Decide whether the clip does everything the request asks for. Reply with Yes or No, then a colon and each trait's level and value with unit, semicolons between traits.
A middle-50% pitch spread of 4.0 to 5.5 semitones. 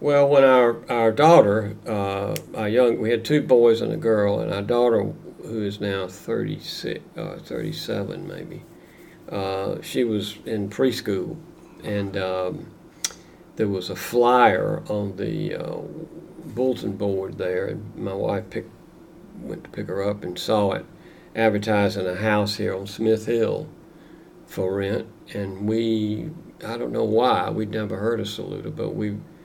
No: average, 2.9 semitones